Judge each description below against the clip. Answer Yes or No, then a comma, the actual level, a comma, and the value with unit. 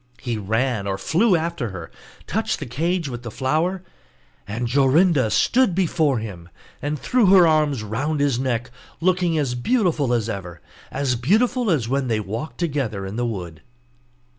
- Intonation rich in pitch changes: Yes, wide, 6.7 semitones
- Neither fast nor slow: Yes, average, 165 wpm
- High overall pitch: No, low, 135 Hz